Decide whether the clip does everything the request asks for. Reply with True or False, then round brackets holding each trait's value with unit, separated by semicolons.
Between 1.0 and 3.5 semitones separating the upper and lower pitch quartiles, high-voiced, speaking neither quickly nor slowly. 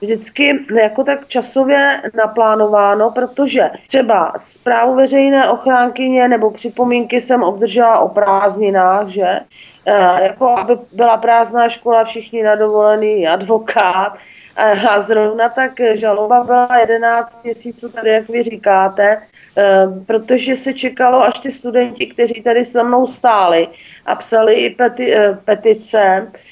True (2.6 semitones; 230 Hz; 125 wpm)